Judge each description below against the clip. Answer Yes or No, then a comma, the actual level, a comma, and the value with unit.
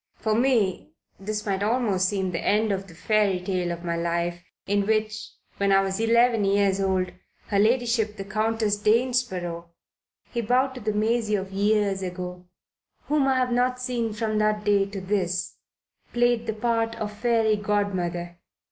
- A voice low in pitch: No, high, 210 Hz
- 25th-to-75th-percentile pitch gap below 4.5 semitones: Yes, average, 3.0 semitones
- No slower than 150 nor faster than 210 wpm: Yes, average, 170 wpm